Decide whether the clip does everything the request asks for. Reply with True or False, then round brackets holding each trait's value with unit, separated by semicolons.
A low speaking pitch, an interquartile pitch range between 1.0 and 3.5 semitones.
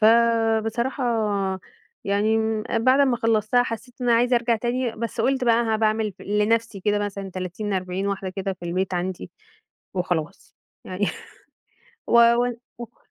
False (220 Hz; 3.1 semitones)